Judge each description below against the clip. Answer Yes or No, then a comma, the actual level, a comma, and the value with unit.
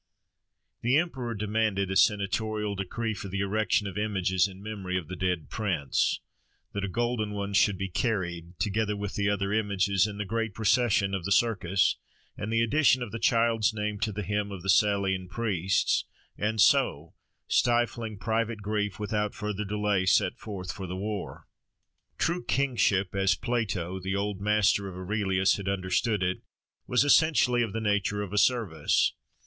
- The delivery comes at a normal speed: Yes, average, 170 wpm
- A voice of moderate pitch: No, low, 105 Hz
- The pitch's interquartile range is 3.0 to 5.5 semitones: No, narrow, 2.5 semitones